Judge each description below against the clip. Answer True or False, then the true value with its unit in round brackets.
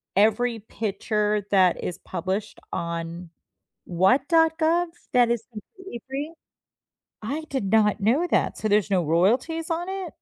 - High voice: True (220 Hz)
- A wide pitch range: True (8.1 semitones)